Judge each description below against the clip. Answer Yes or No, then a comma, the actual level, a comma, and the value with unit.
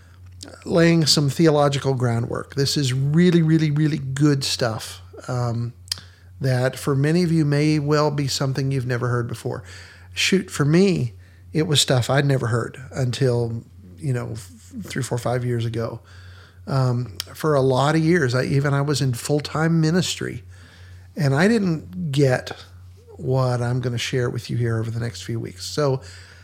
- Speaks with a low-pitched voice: Yes, low, 125 Hz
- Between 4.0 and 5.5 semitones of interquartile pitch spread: Yes, average, 4.8 semitones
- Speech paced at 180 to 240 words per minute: No, average, 170 wpm